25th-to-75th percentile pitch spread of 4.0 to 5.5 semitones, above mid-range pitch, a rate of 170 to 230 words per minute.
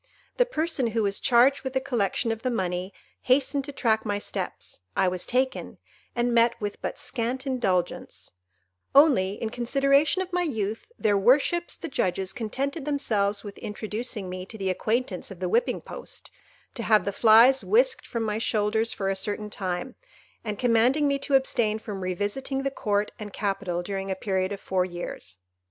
Yes: average, 4.8 semitones; high, 225 Hz; average, 175 wpm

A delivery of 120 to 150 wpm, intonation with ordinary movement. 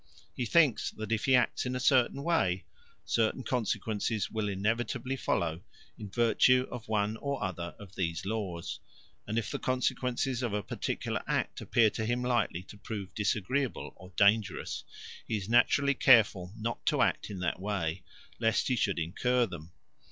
No: average, 165 wpm; average, 4.1 semitones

